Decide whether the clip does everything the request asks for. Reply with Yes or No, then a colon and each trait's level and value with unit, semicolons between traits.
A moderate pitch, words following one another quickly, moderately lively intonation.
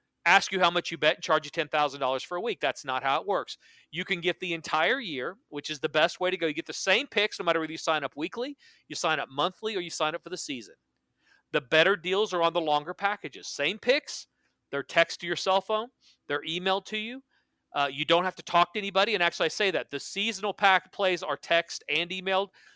Yes: medium, 175 Hz; fast, 250 wpm; average, 3.8 semitones